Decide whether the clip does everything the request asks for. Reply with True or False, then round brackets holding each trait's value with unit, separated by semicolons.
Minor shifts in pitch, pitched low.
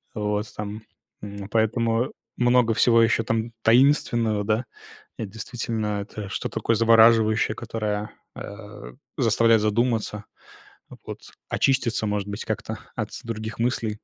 True (1.7 semitones; 110 Hz)